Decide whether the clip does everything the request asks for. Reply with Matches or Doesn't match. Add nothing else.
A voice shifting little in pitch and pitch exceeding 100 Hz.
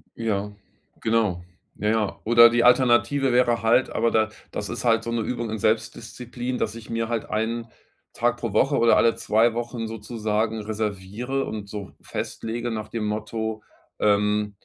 Matches